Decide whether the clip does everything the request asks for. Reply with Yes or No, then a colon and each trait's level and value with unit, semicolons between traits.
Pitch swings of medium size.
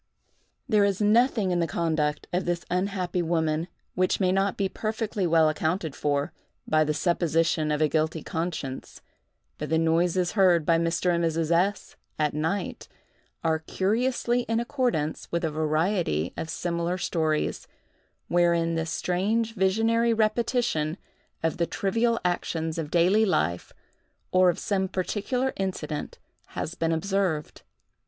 Yes: average, 3.7 semitones